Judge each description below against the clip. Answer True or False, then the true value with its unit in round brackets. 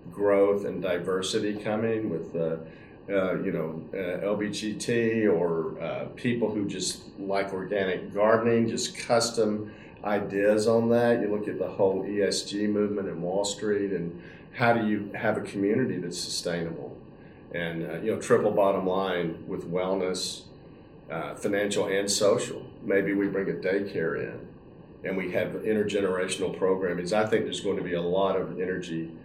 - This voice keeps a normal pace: True (160 wpm)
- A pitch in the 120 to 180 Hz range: False (100 Hz)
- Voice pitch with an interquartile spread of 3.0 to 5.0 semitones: False (2.5 semitones)